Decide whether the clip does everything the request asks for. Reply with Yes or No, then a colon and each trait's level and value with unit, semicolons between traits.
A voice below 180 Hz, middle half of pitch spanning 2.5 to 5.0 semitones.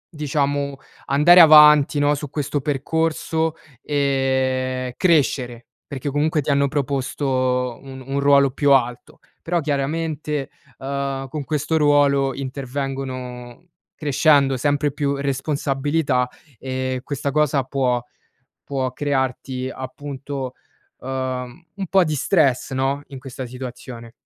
No: medium, 140 Hz; narrow, 2.1 semitones